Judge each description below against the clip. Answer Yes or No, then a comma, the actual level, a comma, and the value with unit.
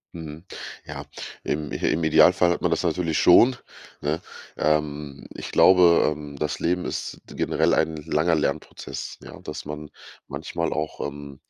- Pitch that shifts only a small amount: Yes, narrow, 2.2 semitones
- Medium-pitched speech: No, very low, 80 Hz